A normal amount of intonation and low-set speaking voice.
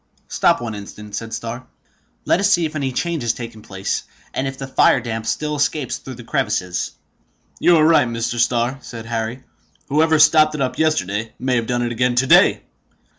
Yes: average, 4.6 semitones; low, 125 Hz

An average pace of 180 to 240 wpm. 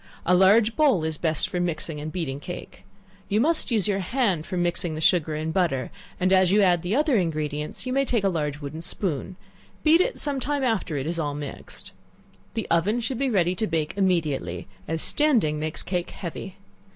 Yes: average, 200 wpm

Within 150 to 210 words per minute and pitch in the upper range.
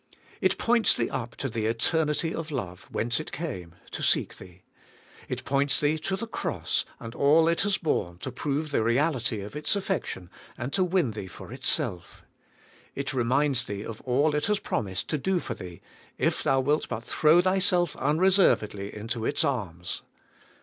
No: average, 175 wpm; low, 135 Hz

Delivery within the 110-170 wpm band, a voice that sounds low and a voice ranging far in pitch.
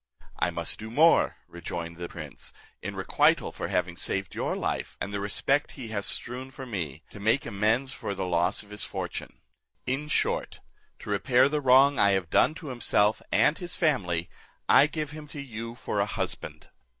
No: average, 185 wpm; low, 110 Hz; wide, 6.0 semitones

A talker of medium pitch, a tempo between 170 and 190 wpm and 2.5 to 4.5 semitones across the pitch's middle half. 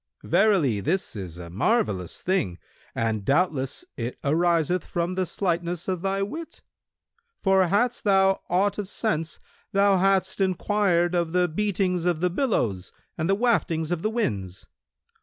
No: medium, 180 Hz; average, 145 wpm; average, 3.9 semitones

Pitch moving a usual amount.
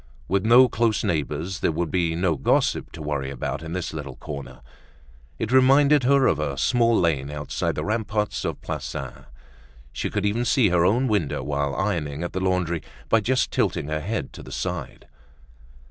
No: wide, 7.1 semitones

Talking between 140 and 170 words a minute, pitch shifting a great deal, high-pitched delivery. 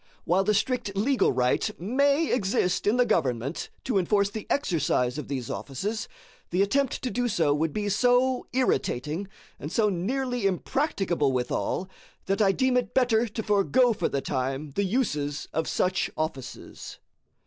Yes: average, 160 wpm; wide, 8.3 semitones; high, 200 Hz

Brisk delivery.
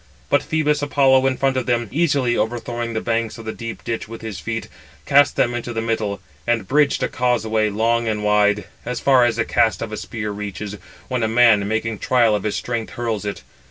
Yes: fast, 215 wpm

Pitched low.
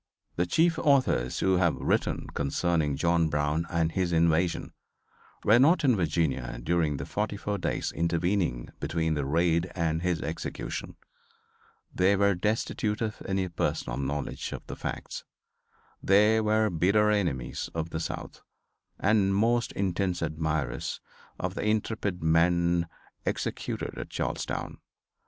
Yes: very low, 85 Hz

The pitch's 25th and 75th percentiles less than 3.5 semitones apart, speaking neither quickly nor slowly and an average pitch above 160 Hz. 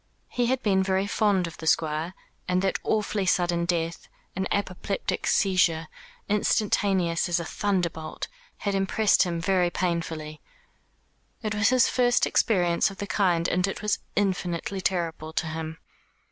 Yes: average, 3.1 semitones; average, 145 wpm; medium, 185 Hz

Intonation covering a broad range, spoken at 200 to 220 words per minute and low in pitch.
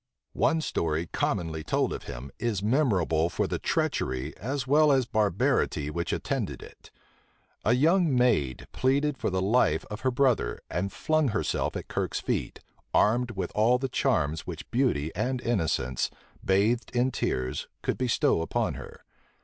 No: wide, 7.6 semitones; average, 155 wpm; low, 110 Hz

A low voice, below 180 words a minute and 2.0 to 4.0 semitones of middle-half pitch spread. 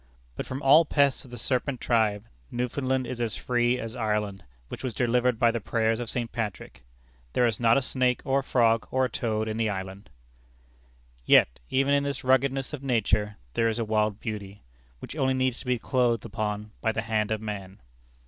No: low, 115 Hz; average, 200 wpm; average, 3.1 semitones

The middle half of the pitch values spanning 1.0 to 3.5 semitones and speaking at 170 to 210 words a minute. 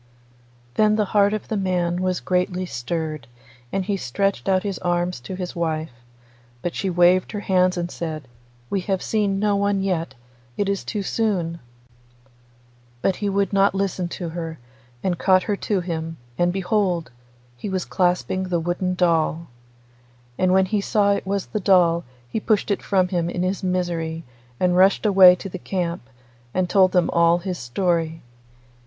Yes: narrow, 2.4 semitones; average, 175 wpm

